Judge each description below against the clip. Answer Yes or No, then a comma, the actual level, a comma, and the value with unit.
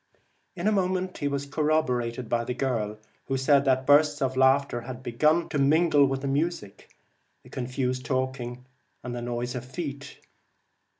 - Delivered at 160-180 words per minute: Yes, average, 165 wpm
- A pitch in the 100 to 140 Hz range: Yes, low, 135 Hz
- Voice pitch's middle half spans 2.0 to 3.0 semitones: Yes, average, 2.7 semitones